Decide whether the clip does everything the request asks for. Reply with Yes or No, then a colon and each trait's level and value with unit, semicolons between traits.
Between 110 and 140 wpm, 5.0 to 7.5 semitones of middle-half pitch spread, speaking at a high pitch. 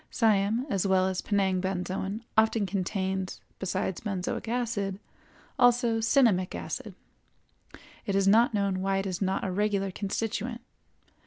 No: slow, 135 wpm; average, 2.8 semitones; high, 195 Hz